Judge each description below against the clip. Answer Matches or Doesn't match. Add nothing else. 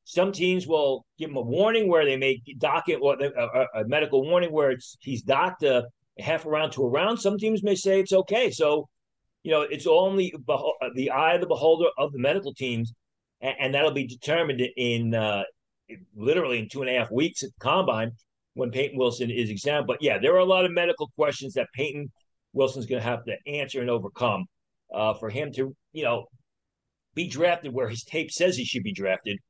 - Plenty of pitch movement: Doesn't match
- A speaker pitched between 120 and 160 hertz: Matches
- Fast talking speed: Matches